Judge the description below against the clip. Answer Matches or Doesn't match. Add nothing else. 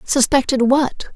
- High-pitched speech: Matches